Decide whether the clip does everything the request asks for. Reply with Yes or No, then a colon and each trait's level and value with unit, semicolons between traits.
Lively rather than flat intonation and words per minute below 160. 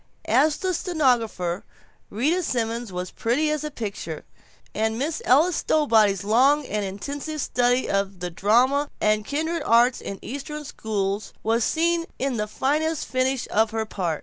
Yes: wide, 6.0 semitones; average, 150 wpm